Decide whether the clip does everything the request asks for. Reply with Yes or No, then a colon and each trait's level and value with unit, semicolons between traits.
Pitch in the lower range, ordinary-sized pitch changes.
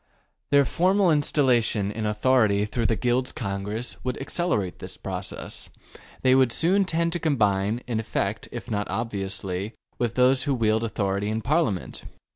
Yes: low, 115 Hz; average, 4.4 semitones